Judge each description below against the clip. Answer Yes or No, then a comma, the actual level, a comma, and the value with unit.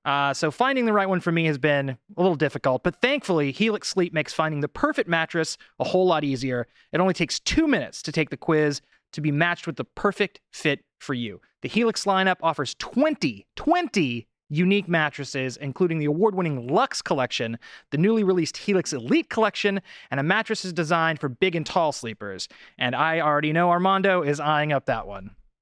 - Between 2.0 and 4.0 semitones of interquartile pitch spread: No, average, 4.9 semitones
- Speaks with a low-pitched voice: No, medium, 165 Hz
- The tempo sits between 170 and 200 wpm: Yes, average, 190 wpm